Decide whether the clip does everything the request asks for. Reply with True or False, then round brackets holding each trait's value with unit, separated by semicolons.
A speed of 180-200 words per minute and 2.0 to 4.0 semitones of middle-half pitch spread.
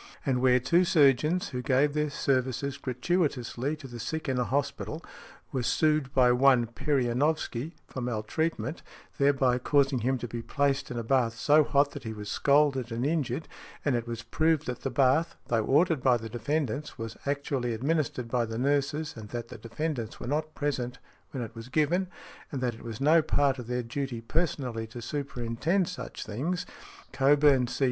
True (185 wpm; 3.7 semitones)